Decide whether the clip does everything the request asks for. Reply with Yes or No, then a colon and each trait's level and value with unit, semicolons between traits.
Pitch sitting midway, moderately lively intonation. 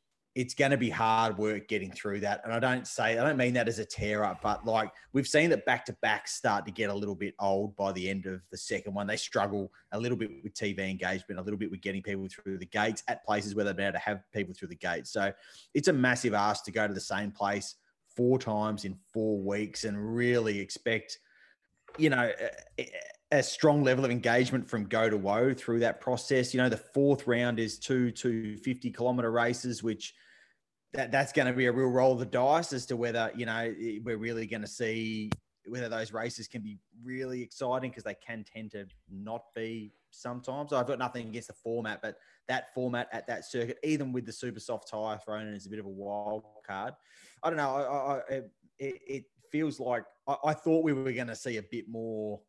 No: low, 115 Hz; average, 3.2 semitones